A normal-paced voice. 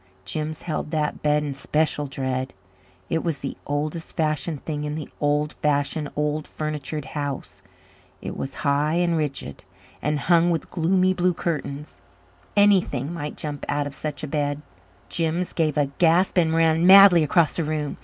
Yes: average, 165 wpm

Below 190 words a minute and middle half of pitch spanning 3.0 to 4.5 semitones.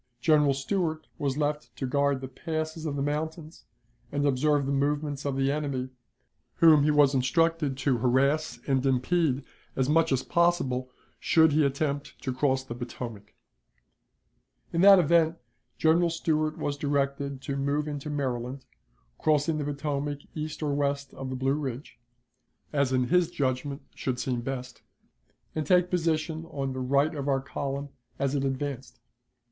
No: average, 155 wpm; narrow, 2.5 semitones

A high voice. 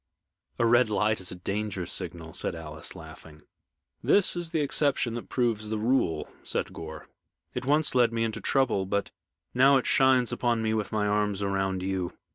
No: low, 110 Hz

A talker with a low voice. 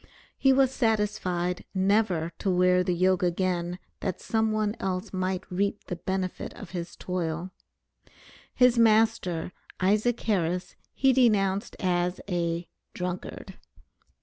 No: medium, 185 Hz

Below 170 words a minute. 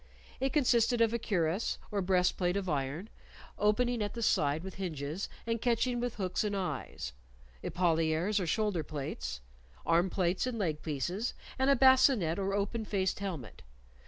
Yes: average, 160 wpm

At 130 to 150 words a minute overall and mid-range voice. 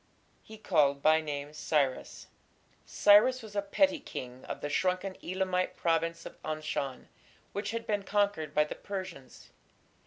Yes: average, 145 wpm; medium, 180 Hz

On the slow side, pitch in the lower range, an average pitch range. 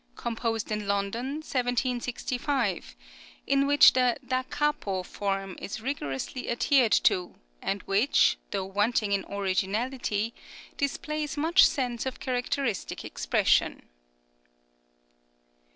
No: slow, 100 wpm; high, 240 Hz; average, 4.9 semitones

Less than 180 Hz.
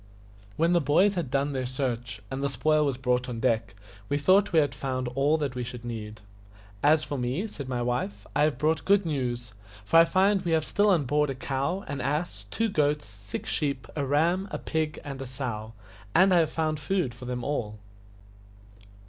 Yes: medium, 140 Hz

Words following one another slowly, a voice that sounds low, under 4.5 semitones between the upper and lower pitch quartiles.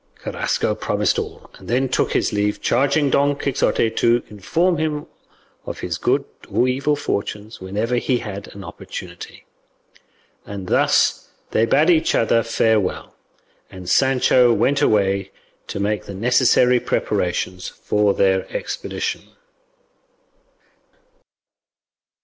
No: slow, 120 wpm; low, 115 Hz; average, 5.0 semitones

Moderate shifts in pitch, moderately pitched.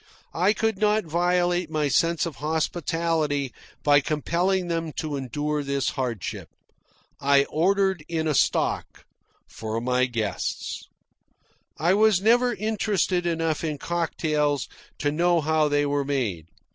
Yes: average, 3.6 semitones; medium, 160 Hz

